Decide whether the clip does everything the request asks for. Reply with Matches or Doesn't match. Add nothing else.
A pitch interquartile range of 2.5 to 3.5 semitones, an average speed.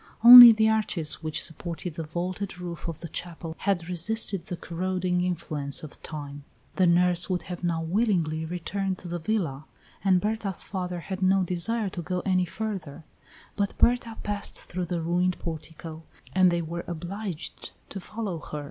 Matches